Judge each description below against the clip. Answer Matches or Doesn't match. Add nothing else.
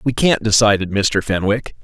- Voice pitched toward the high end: Doesn't match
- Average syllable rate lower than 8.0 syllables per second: Matches